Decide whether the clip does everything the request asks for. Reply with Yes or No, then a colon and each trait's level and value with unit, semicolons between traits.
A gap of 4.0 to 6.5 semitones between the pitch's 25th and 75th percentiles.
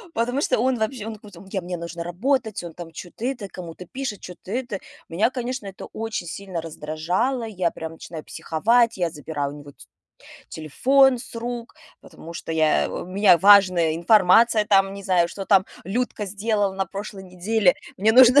Yes: average, 4.9 semitones